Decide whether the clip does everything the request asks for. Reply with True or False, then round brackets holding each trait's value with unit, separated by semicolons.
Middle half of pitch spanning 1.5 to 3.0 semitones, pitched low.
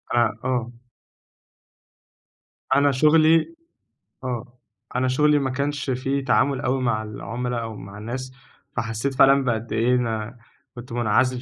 True (2.7 semitones; 125 Hz)